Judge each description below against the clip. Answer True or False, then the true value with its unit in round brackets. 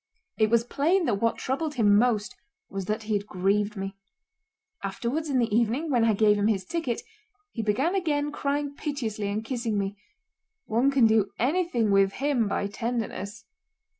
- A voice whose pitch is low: False (225 Hz)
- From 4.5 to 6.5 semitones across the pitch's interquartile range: True (5.2 semitones)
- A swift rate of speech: False (170 wpm)